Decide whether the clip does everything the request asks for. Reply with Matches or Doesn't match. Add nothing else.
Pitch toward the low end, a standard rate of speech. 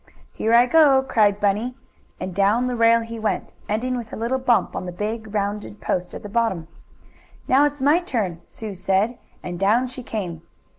Doesn't match